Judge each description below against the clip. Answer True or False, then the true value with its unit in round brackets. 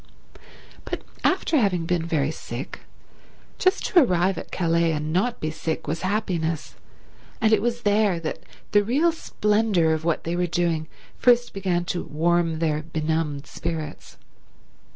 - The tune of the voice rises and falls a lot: False (4.5 semitones)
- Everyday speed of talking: True (150 wpm)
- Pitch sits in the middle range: True (170 Hz)